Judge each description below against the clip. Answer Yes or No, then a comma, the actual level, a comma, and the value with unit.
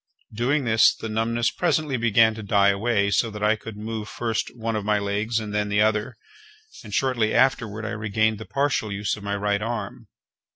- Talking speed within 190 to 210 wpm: Yes, average, 200 wpm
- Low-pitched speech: Yes, low, 110 Hz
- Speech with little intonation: Yes, narrow, 1.9 semitones